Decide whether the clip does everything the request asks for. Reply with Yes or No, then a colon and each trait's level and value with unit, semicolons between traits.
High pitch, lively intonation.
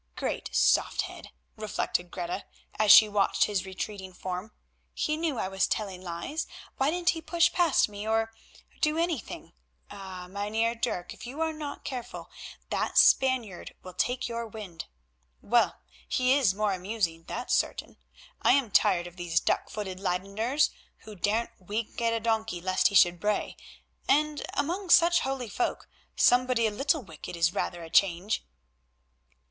Yes: high, 215 Hz; wide, 5.8 semitones